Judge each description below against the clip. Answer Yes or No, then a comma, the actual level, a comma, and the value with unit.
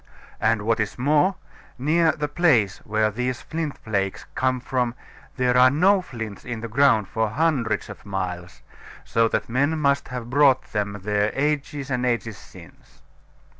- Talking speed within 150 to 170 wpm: Yes, average, 160 wpm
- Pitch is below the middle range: Yes, low, 125 Hz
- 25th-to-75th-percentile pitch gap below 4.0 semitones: No, average, 4.7 semitones